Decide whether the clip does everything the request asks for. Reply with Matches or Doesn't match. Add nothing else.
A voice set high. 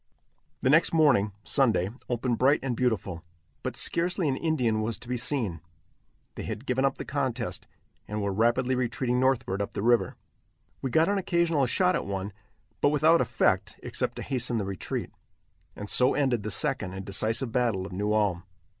Doesn't match